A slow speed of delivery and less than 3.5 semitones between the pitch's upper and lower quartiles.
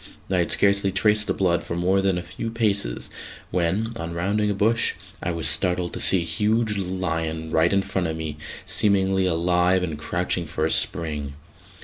No: average, 190 wpm; average, 3.0 semitones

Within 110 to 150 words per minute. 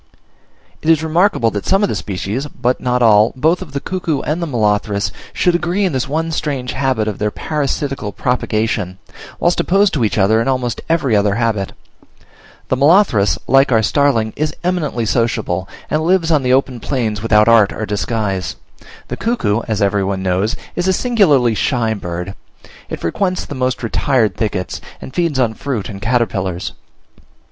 No: average, 170 wpm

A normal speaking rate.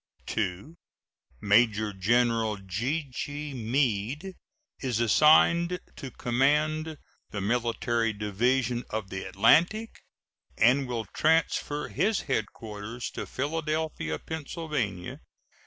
No: slow, 90 wpm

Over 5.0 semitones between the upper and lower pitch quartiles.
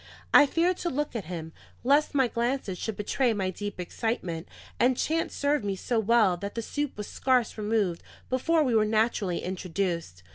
Yes: wide, 5.6 semitones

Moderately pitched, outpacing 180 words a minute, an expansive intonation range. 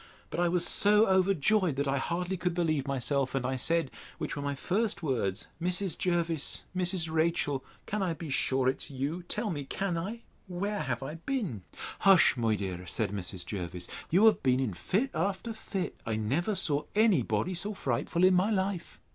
Yes: medium, 165 Hz; average, 190 wpm; wide, 6.2 semitones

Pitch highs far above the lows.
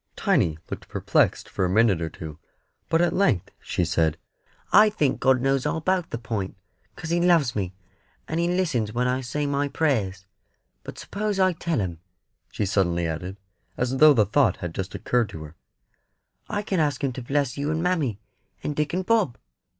Yes: wide, 8.8 semitones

